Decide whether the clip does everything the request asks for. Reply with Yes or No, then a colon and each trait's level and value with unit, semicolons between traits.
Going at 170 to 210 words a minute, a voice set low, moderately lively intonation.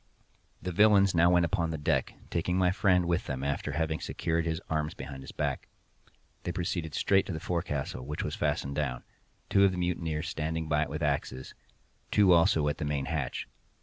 Yes: average, 180 wpm; very low, 80 Hz; average, 3.2 semitones